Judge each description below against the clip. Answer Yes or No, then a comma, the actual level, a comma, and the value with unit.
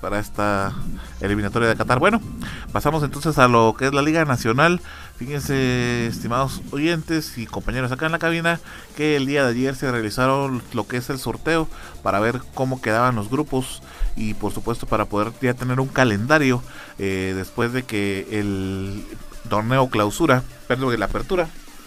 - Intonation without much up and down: No, average, 4.6 semitones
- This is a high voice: No, low, 125 Hz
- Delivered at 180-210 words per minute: No, average, 165 wpm